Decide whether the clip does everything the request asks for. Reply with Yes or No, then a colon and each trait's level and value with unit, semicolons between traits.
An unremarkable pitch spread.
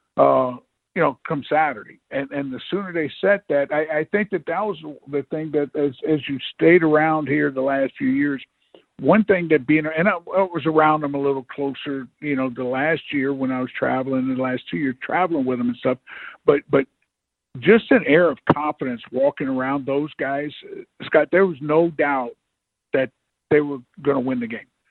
Yes: average, 3.5 semitones